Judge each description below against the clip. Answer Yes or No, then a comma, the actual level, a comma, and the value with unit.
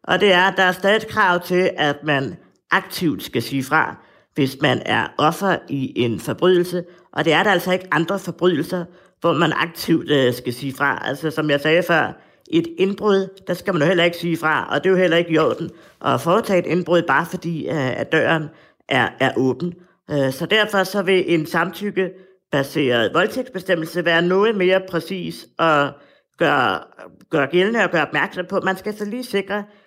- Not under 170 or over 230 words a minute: Yes, average, 190 wpm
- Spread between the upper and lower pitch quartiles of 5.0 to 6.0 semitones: No, average, 3.2 semitones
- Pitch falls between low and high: Yes, medium, 175 Hz